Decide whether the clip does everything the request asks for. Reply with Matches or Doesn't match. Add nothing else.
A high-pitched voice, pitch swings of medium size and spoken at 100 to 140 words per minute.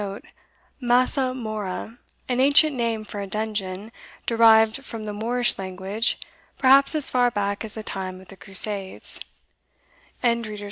Matches